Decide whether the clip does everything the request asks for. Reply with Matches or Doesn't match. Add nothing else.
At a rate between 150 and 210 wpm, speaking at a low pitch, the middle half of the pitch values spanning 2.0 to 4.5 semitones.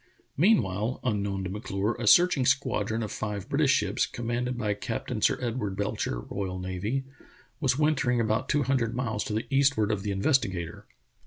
Matches